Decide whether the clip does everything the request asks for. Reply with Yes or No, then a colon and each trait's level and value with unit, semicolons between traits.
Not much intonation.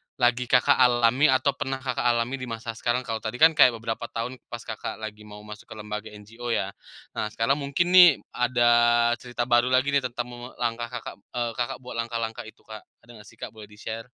Yes: narrow, 2.1 semitones